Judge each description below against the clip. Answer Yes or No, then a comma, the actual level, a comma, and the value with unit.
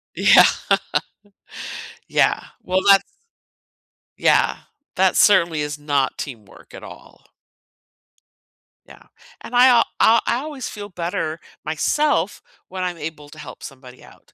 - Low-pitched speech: No, medium, 170 Hz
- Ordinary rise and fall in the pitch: No, wide, 5.8 semitones